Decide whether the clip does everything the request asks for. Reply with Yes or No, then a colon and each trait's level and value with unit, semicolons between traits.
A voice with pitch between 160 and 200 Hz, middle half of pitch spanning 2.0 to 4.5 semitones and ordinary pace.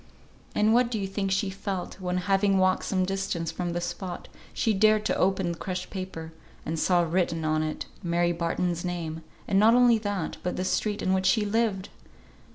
Yes: medium, 185 Hz; narrow, 2.6 semitones; average, 195 wpm